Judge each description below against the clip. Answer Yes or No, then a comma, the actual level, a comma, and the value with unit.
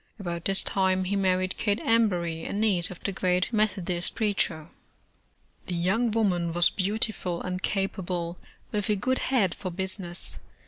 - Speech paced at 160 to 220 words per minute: No, average, 150 wpm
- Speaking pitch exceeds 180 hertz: Yes, high, 190 Hz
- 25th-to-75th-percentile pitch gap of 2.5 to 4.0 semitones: Yes, average, 2.8 semitones